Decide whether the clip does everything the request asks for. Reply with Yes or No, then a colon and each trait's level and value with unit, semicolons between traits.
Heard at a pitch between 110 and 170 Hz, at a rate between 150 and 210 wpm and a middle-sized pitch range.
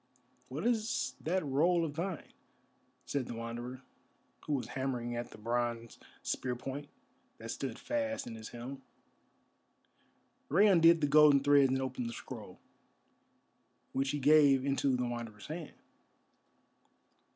No: low, 135 Hz; slow, 135 wpm; average, 4.2 semitones